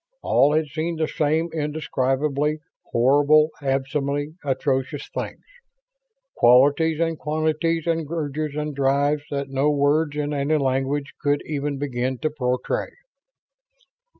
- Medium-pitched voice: Yes, medium, 145 Hz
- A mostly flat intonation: Yes, narrow, 2.0 semitones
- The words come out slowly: Yes, slow, 120 wpm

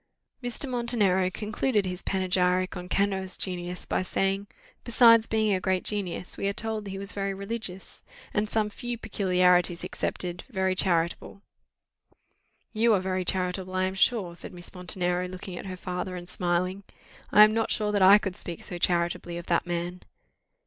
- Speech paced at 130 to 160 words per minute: No, average, 170 wpm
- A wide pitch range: No, narrow, 2.5 semitones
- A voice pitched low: No, high, 190 Hz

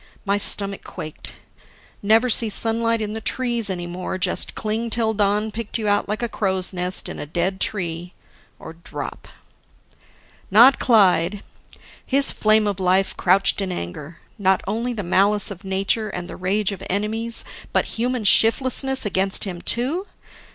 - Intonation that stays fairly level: No, average, 3.2 semitones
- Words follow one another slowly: No, average, 160 wpm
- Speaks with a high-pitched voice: Yes, high, 205 Hz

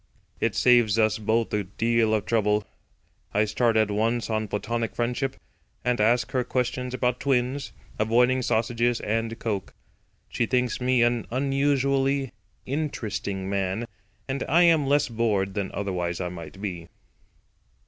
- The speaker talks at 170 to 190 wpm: No, average, 140 wpm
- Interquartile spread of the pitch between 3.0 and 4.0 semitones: Yes, average, 3.3 semitones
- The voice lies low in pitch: Yes, low, 115 Hz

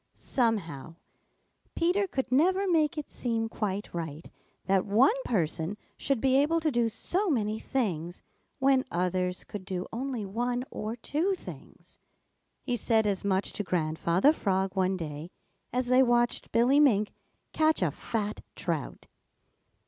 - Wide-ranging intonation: Yes, wide, 6.2 semitones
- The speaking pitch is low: No, high, 225 Hz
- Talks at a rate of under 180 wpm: Yes, average, 140 wpm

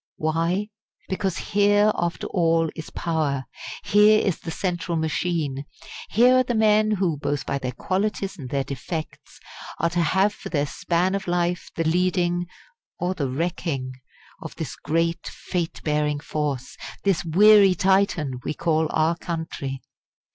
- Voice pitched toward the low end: No, medium, 170 Hz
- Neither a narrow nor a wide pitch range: Yes, average, 3.8 semitones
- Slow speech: No, average, 145 wpm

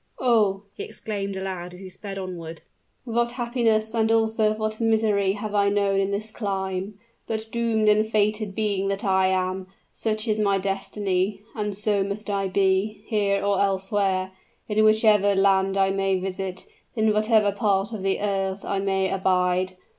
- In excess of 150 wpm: Yes, average, 165 wpm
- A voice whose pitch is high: Yes, high, 200 Hz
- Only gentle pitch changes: Yes, narrow, 2.0 semitones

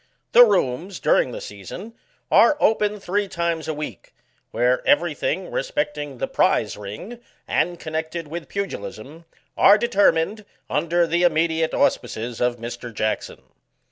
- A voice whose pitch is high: No, medium, 165 Hz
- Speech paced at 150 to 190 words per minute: No, slow, 135 wpm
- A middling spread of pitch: No, wide, 8.2 semitones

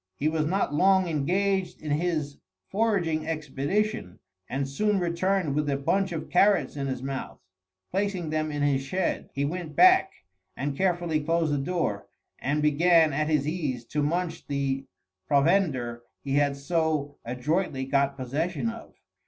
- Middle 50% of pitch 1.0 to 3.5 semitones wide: No, average, 4.3 semitones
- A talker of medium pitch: Yes, medium, 155 Hz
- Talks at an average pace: Yes, average, 155 wpm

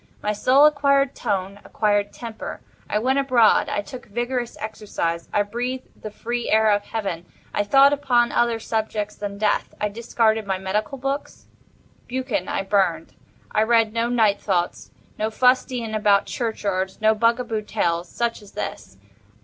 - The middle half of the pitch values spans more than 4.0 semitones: No, average, 3.0 semitones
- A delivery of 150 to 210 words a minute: No, average, 140 wpm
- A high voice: Yes, high, 220 Hz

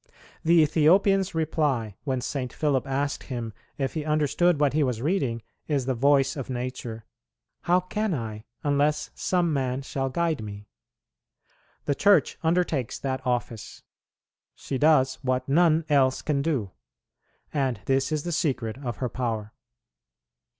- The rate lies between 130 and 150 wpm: Yes, average, 145 wpm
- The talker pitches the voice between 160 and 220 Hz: No, medium, 140 Hz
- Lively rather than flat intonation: No, average, 3.6 semitones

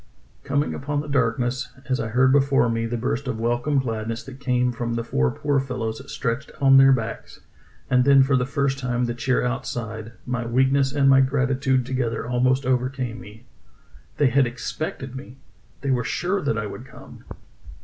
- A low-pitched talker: Yes, low, 130 Hz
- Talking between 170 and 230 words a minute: Yes, average, 180 wpm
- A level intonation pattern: Yes, narrow, 2.2 semitones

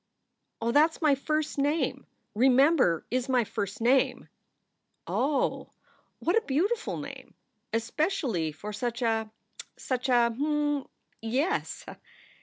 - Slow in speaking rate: Yes, slow, 115 wpm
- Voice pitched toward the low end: No, very high, 260 Hz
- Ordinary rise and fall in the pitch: Yes, average, 4.6 semitones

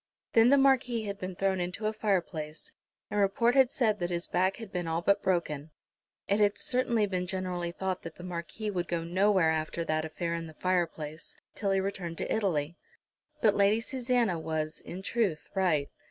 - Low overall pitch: No, medium, 185 Hz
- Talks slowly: No, average, 190 wpm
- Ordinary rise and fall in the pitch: Yes, average, 3.8 semitones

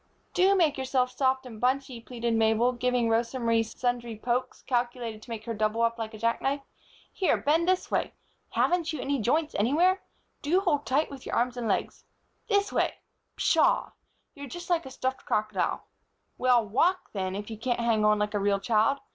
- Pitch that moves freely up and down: No, average, 3.9 semitones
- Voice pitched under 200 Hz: No, high, 245 Hz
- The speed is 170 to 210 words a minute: Yes, average, 190 wpm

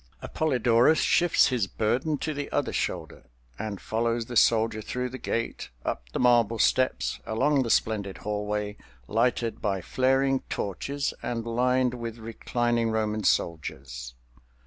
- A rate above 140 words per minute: No, slow, 135 wpm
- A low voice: Yes, low, 115 Hz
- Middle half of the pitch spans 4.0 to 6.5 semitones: No, average, 2.9 semitones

